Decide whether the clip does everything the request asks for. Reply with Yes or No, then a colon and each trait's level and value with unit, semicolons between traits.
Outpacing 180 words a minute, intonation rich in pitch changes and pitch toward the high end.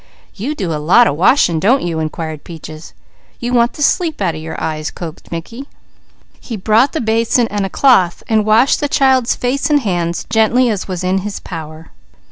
Yes: average, 190 wpm; wide, 6.7 semitones; high, 205 Hz